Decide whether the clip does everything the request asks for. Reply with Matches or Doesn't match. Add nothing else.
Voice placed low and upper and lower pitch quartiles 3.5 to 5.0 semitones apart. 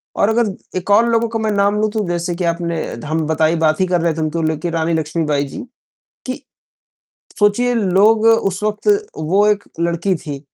Doesn't match